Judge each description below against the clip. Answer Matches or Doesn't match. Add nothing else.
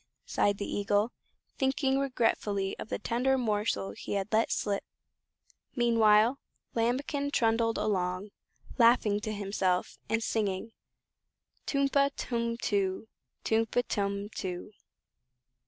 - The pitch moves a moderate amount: Matches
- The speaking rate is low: Matches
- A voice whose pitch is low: Doesn't match